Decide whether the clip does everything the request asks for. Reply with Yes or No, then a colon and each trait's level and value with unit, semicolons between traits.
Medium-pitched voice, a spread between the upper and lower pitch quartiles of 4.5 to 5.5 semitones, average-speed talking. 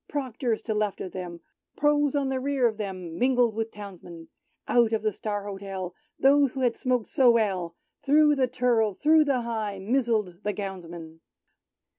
No: high, 220 Hz; average, 5.0 semitones; average, 170 wpm